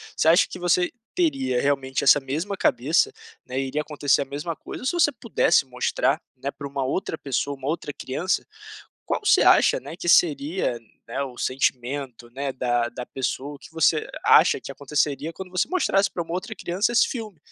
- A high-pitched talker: No, medium, 145 Hz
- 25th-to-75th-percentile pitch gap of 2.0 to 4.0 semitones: No, average, 5.1 semitones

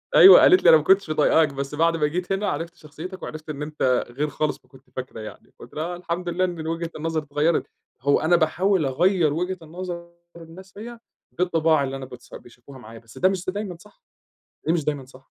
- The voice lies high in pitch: No, medium, 160 Hz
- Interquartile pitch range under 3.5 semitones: No, average, 3.8 semitones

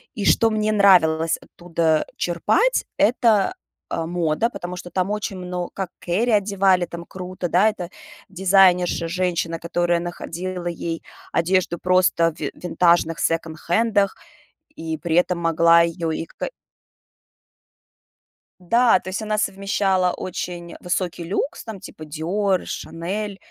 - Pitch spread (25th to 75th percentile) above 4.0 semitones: No, average, 2.7 semitones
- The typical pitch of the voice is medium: Yes, medium, 180 Hz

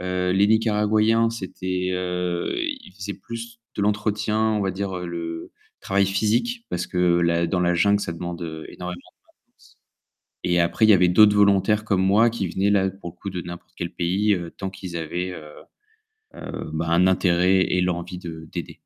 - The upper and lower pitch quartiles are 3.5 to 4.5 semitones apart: No, average, 3.0 semitones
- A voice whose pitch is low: Yes, very low, 95 Hz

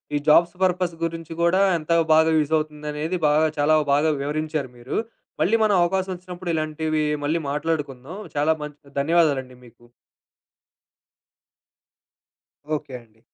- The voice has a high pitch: No, medium, 155 Hz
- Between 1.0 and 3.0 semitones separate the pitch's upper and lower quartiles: Yes, narrow, 2.4 semitones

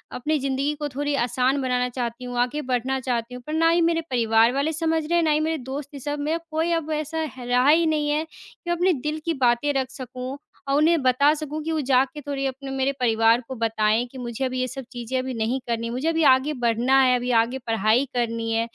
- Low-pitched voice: No, very high, 265 Hz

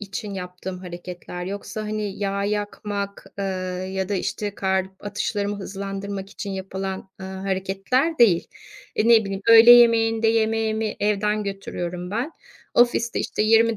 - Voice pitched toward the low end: No, high, 200 Hz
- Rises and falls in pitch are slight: Yes, narrow, 2.3 semitones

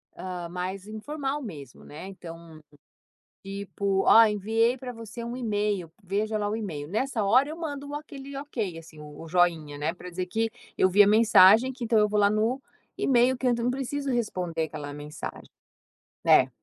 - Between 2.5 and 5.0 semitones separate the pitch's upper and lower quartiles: No, wide, 5.4 semitones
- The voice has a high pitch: Yes, high, 210 Hz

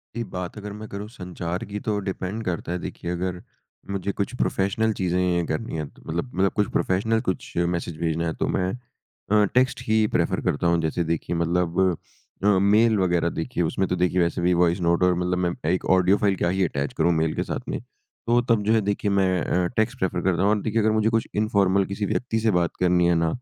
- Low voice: Yes, very low, 95 Hz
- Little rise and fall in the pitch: No, average, 3.3 semitones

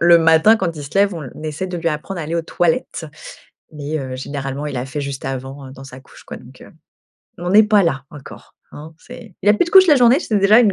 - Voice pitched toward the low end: No, medium, 160 Hz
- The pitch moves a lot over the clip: Yes, wide, 6.0 semitones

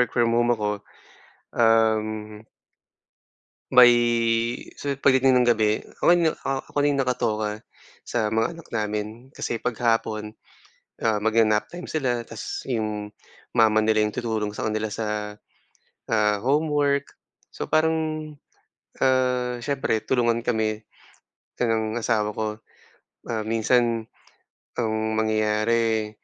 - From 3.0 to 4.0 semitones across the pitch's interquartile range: No, narrow, 2.6 semitones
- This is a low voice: Yes, low, 115 Hz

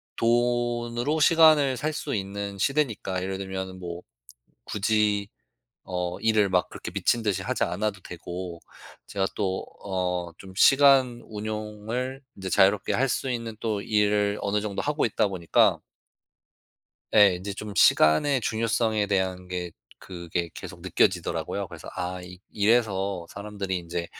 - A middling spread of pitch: Yes, average, 3.8 semitones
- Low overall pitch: Yes, low, 100 Hz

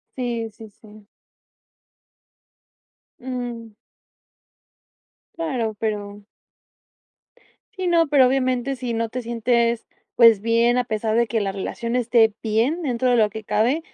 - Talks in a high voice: Yes, high, 235 Hz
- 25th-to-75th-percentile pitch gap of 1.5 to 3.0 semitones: Yes, narrow, 2.4 semitones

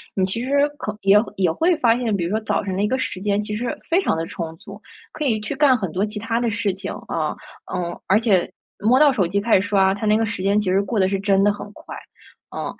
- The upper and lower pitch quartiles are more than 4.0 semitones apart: No, average, 3.1 semitones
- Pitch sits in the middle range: No, high, 205 Hz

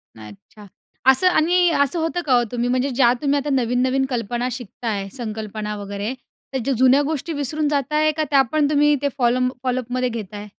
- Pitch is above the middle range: Yes, very high, 255 Hz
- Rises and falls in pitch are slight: No, average, 3.7 semitones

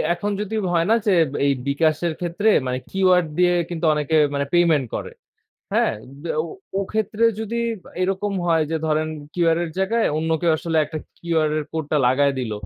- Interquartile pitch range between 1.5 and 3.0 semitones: No, average, 3.5 semitones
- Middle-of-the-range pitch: Yes, medium, 170 Hz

